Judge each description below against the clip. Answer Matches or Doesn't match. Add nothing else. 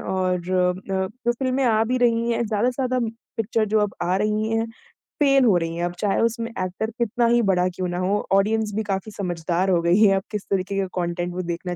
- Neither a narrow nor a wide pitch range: Matches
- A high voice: Matches